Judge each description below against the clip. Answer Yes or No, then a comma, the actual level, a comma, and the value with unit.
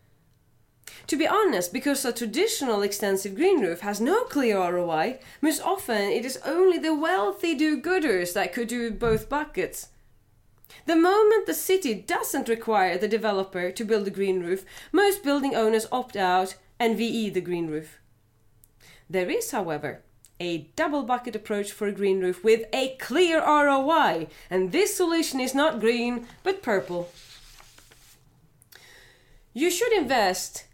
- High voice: Yes, high, 225 Hz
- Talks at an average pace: Yes, average, 150 wpm